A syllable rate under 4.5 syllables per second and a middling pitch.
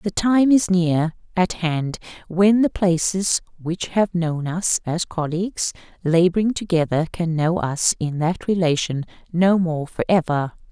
Yes: 4.1 syllables/s; medium, 175 Hz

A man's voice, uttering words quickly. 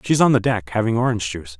Yes: male; fast, 265 wpm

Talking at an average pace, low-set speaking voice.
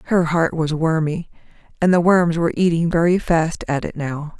No: average, 190 wpm; medium, 165 Hz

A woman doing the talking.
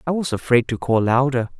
No: male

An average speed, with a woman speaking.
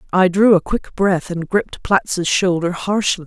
Yes: average, 185 wpm; female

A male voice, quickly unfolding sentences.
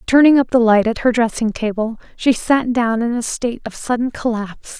No: female; fast, 215 wpm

